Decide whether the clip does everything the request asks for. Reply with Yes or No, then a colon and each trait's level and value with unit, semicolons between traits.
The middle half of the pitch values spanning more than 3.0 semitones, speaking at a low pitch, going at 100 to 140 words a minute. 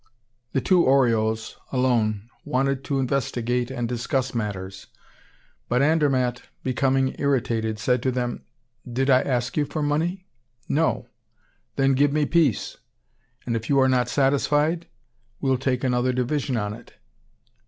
No: narrow, 2.5 semitones; low, 130 Hz; slow, 135 wpm